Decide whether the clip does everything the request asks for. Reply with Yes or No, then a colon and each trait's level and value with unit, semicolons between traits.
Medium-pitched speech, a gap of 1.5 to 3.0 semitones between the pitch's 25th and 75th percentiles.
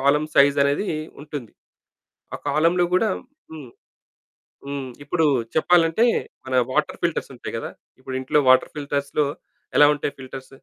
Yes: medium, 145 Hz; average, 2.7 semitones